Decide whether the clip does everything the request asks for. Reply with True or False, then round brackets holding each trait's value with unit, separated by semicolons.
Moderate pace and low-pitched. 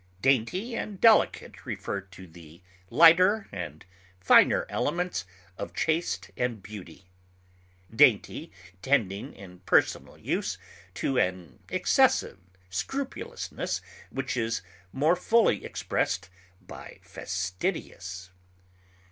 False (95 wpm; 105 Hz)